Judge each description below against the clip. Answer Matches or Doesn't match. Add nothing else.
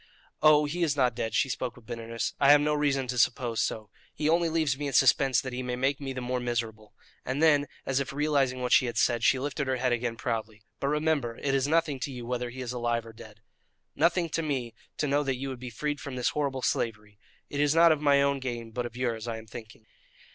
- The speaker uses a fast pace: Matches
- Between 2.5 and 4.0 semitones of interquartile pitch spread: Matches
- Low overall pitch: Matches